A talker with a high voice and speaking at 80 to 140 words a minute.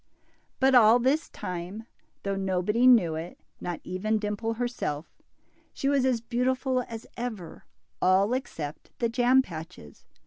Yes: high, 225 Hz; slow, 135 wpm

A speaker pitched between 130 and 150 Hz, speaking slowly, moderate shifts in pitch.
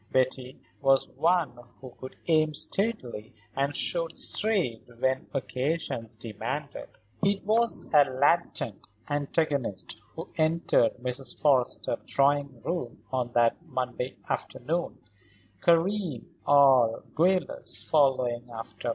Yes: medium, 140 Hz; slow, 105 wpm; average, 4.7 semitones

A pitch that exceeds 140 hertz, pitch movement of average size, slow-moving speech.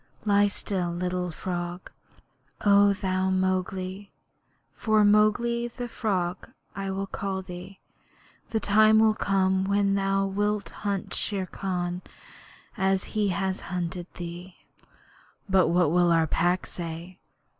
No: high, 190 Hz; narrow, 2.1 semitones; slow, 125 wpm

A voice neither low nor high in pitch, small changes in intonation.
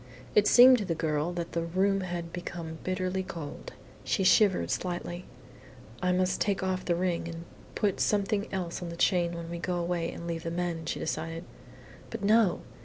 Yes: medium, 175 Hz; narrow, 2.1 semitones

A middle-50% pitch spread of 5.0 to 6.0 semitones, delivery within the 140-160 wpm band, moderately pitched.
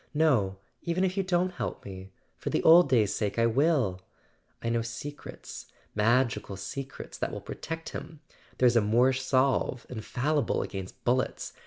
No: wide, 5.6 semitones; average, 150 wpm; low, 125 Hz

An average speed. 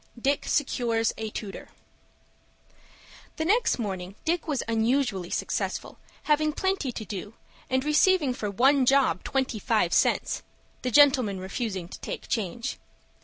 No: slow, 125 wpm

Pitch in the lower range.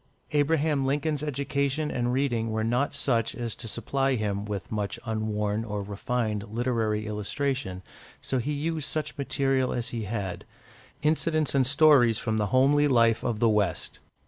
Yes: low, 120 Hz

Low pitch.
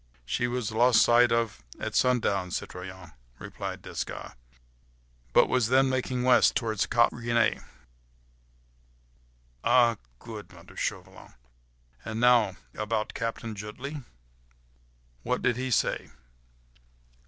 Yes: low, 115 Hz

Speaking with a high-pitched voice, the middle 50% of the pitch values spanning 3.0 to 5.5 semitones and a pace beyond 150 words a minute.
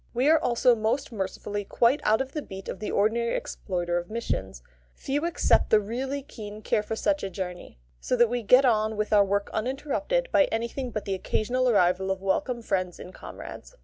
Yes: high, 220 Hz; average, 4.6 semitones; average, 200 wpm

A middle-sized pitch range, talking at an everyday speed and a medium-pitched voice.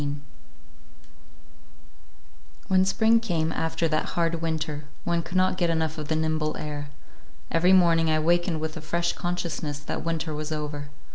No: narrow, 2.0 semitones; average, 155 wpm; medium, 160 Hz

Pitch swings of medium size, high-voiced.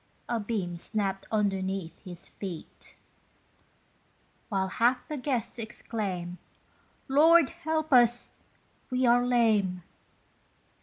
Yes: average, 4.7 semitones; high, 220 Hz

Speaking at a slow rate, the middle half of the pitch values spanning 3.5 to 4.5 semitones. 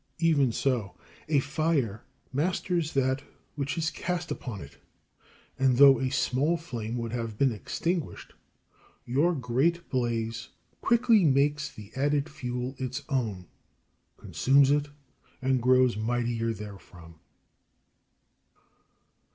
Yes: slow, 110 wpm; average, 4.1 semitones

